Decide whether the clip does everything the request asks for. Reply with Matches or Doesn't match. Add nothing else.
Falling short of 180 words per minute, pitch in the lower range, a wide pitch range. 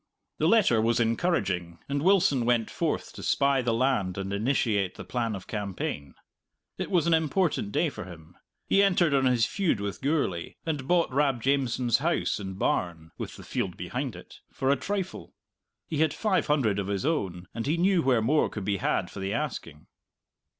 Doesn't match